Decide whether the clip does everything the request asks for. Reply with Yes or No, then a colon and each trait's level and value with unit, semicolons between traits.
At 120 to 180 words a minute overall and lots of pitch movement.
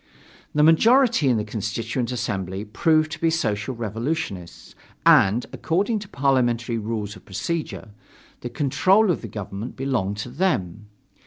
Yes: average, 140 wpm; wide, 7.0 semitones